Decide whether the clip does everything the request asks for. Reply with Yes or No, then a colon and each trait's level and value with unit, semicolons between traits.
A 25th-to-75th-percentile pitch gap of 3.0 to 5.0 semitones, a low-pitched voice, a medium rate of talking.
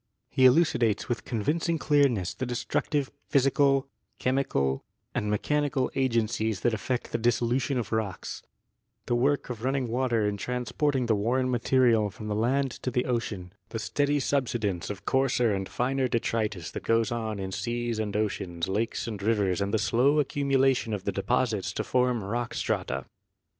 Yes: average, 3.8 semitones; low, 120 Hz; average, 165 wpm